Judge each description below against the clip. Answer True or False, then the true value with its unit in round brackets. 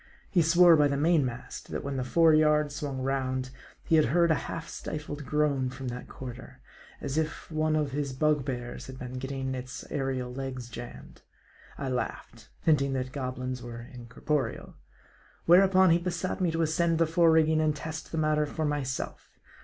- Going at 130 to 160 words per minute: False (180 wpm)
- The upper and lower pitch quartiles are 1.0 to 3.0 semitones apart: False (3.6 semitones)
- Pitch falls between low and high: True (145 Hz)